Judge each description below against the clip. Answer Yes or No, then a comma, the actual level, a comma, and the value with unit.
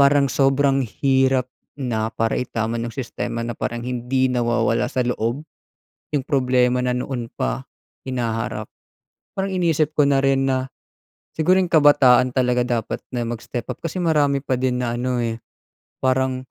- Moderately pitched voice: No, low, 130 Hz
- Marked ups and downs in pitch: No, narrow, 2.4 semitones